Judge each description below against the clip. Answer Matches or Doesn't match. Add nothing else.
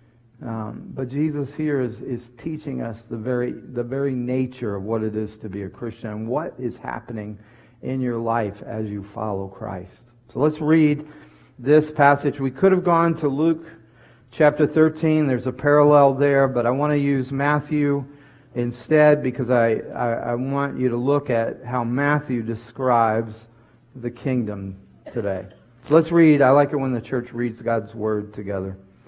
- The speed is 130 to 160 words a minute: Doesn't match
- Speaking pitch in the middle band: Doesn't match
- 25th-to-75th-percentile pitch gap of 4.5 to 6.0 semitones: Doesn't match